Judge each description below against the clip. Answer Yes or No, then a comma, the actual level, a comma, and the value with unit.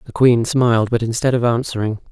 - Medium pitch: No, low, 120 Hz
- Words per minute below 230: Yes, average, 200 wpm